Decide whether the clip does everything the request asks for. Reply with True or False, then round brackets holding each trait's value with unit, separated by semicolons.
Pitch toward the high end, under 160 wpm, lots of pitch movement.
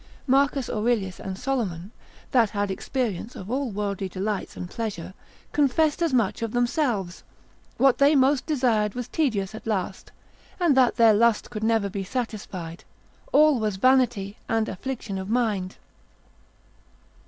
False (225 Hz; 140 wpm; 4.7 semitones)